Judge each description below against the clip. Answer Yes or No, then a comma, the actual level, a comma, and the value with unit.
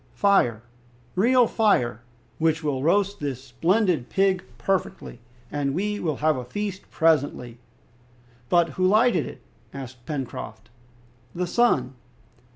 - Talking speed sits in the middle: No, slow, 120 wpm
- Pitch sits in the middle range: Yes, medium, 160 Hz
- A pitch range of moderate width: No, wide, 7.0 semitones